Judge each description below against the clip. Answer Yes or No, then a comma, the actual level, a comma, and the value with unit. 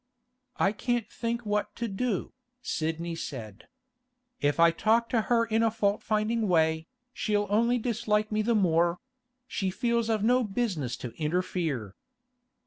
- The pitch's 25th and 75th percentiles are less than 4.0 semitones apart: No, wide, 5.5 semitones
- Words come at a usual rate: Yes, average, 145 wpm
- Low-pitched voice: No, high, 210 Hz